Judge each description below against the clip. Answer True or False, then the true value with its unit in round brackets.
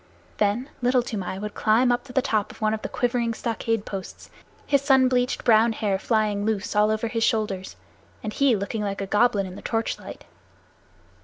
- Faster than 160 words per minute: True (200 wpm)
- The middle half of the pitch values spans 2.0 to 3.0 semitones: True (2.7 semitones)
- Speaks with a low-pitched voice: False (220 Hz)